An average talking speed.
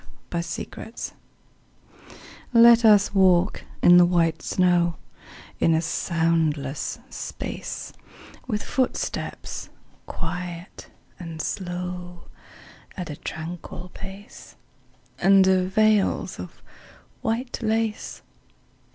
No: slow, 85 wpm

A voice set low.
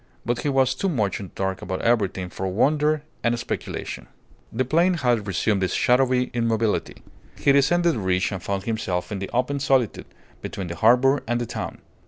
Yes: low, 120 Hz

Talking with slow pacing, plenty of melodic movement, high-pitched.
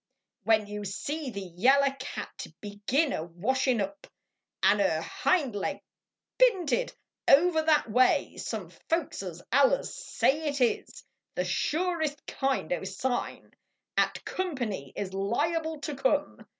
Yes: slow, 125 wpm; wide, 7.4 semitones; very high, 265 Hz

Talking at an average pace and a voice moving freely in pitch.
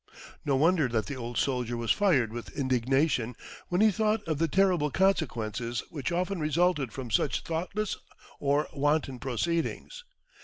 Yes: average, 150 wpm; wide, 6.1 semitones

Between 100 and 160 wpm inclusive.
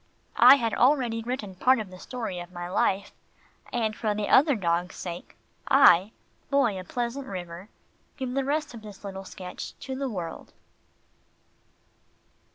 Yes: average, 155 wpm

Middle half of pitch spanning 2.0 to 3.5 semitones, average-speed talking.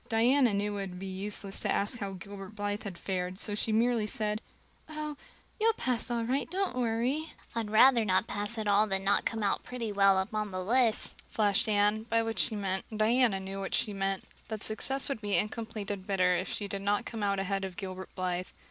No: average, 2.7 semitones; fast, 220 wpm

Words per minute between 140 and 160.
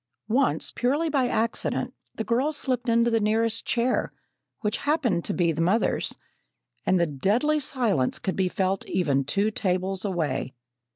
Yes: average, 155 wpm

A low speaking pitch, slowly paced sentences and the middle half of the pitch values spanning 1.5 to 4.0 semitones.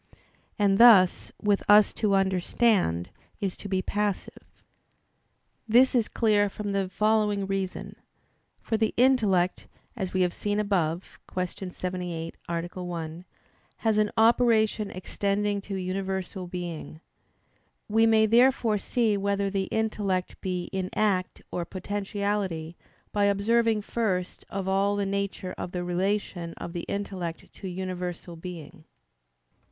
No: high, 195 Hz; slow, 130 wpm; narrow, 2.5 semitones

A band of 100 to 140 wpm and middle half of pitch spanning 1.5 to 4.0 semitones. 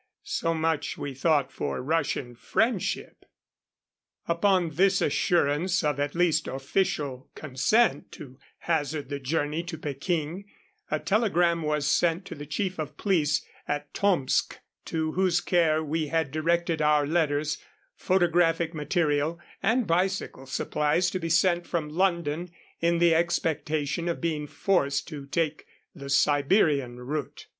Yes: slow, 135 wpm; average, 3.0 semitones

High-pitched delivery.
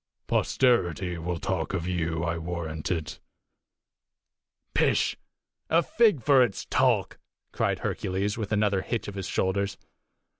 No: very low, 95 Hz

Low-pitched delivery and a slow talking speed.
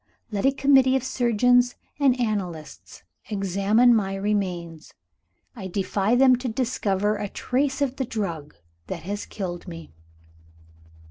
No: high, 210 Hz; slow, 130 wpm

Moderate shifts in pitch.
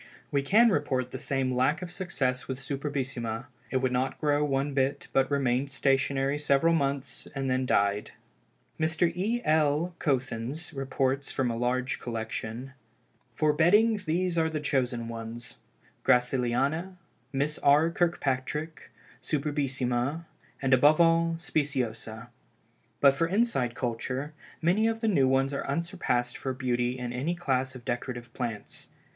Yes: average, 3.9 semitones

